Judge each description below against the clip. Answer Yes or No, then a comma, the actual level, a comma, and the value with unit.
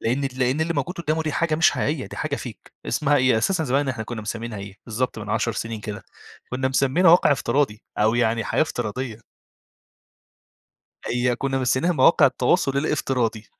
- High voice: No, low, 130 Hz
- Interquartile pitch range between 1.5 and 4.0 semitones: No, average, 4.4 semitones